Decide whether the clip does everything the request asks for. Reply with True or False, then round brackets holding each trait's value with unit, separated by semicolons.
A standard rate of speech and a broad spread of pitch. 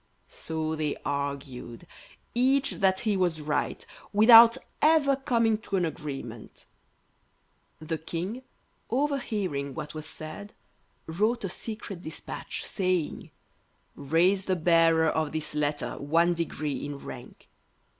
False (115 wpm; 5.9 semitones)